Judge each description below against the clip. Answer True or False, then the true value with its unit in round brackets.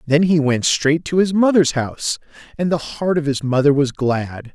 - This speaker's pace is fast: True (210 wpm)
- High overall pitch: False (150 Hz)